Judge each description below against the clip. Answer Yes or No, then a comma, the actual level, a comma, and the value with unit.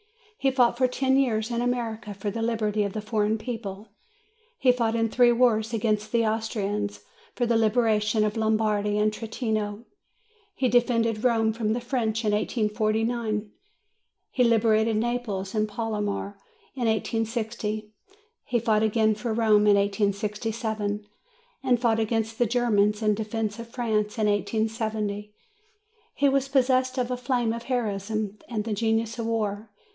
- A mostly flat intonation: Yes, narrow, 1.9 semitones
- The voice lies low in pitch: No, high, 220 Hz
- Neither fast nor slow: Yes, average, 150 wpm